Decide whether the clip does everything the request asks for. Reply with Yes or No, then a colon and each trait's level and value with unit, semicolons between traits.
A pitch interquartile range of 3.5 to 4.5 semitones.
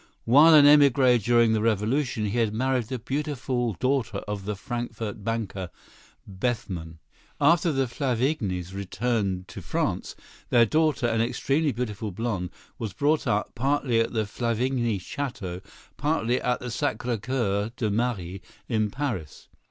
Yes: average, 4.1 semitones